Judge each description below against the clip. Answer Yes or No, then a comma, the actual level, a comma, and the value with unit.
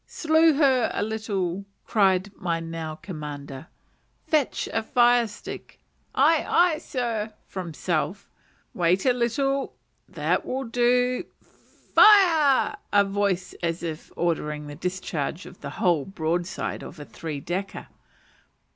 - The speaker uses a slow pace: Yes, slow, 130 wpm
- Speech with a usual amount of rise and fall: No, wide, 6.8 semitones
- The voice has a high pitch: Yes, high, 195 Hz